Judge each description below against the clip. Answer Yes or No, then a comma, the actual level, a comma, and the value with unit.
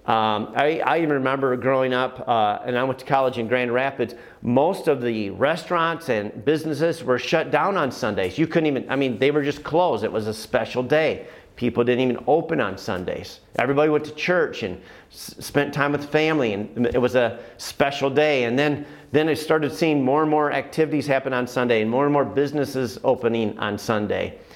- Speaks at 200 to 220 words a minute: Yes, fast, 205 wpm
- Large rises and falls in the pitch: No, average, 3.4 semitones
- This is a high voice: No, low, 135 Hz